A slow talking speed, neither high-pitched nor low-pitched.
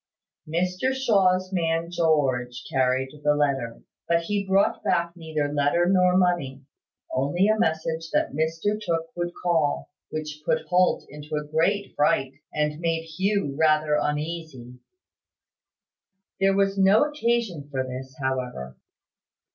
Yes: slow, 130 wpm; medium, 160 Hz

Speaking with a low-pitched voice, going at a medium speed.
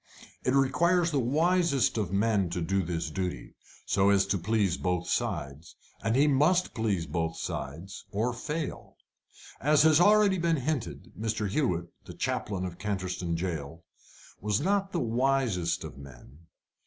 Yes: low, 105 Hz; average, 150 wpm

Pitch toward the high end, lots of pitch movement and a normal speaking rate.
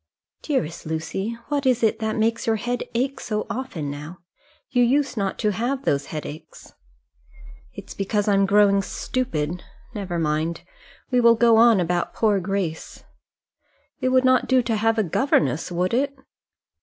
Yes: high, 215 Hz; wide, 5.8 semitones; average, 155 wpm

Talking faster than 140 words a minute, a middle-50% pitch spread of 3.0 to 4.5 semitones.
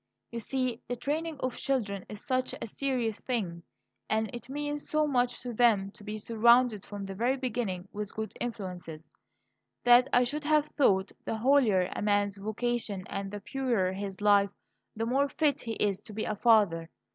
Yes: average, 180 wpm; average, 4.0 semitones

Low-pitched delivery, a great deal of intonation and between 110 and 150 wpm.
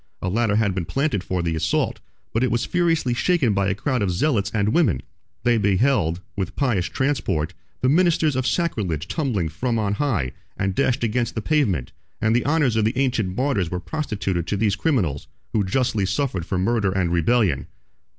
No: low, 110 Hz; wide, 6.0 semitones; average, 190 wpm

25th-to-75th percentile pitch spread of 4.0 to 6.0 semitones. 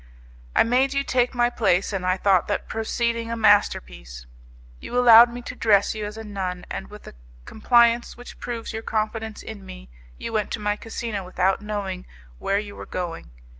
No: average, 3.3 semitones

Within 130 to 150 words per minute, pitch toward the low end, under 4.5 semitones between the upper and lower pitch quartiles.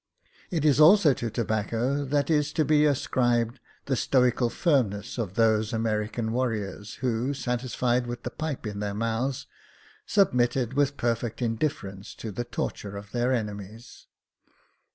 Yes: average, 145 wpm; low, 120 Hz; average, 3.6 semitones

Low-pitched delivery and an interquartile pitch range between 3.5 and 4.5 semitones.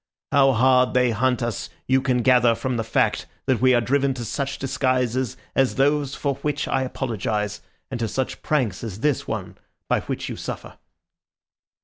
No: low, 130 Hz; narrow, 2.4 semitones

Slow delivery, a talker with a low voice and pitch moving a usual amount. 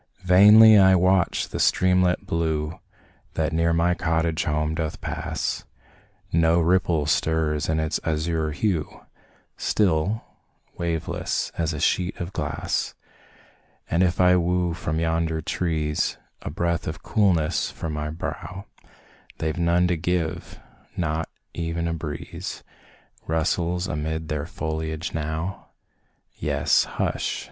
No: slow, 120 wpm; very low, 85 Hz; narrow, 2.1 semitones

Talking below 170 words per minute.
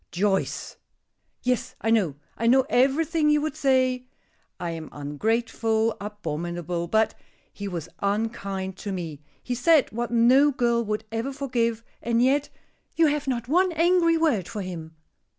Yes: average, 150 wpm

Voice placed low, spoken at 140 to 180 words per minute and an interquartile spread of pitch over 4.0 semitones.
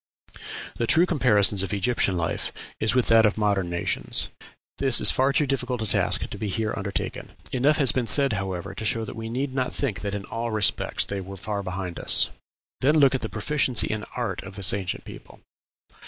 No: low, 110 Hz; fast, 205 wpm; average, 4.5 semitones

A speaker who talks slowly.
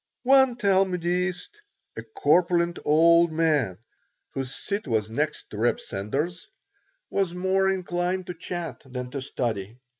Yes: slow, 125 wpm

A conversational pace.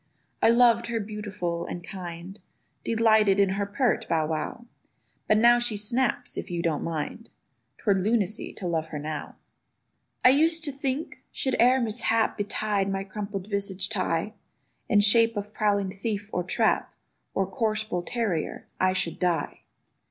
Yes: average, 150 wpm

